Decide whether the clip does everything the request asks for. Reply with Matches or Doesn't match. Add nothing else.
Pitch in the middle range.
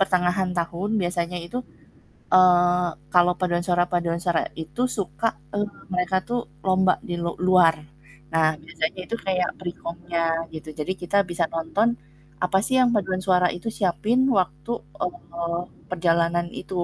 Matches